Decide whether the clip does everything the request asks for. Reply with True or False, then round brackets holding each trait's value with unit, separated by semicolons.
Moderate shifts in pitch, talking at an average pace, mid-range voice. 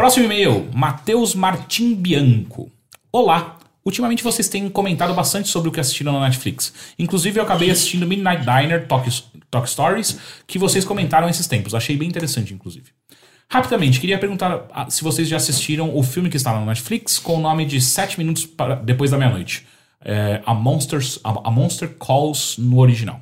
False (6.1 semitones; 175 wpm; 155 Hz)